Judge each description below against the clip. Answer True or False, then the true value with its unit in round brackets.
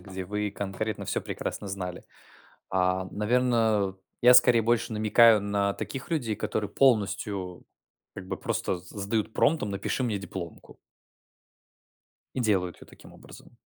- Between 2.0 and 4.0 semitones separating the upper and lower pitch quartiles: True (3.1 semitones)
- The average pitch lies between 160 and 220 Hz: False (105 Hz)